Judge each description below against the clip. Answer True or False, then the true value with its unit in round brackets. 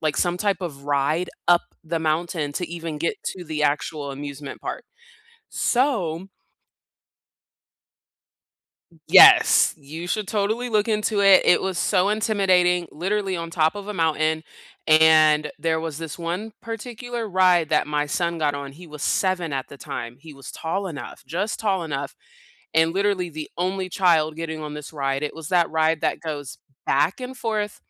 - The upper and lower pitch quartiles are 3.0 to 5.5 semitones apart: True (4.0 semitones)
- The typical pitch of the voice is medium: True (165 Hz)